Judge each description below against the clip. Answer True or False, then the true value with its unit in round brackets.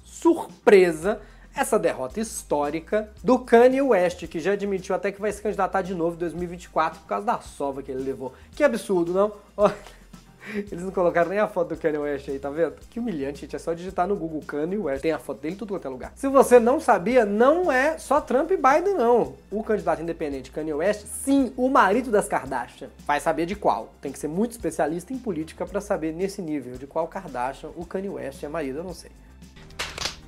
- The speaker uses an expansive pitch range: True (6.0 semitones)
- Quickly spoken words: True (210 wpm)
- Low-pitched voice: False (185 Hz)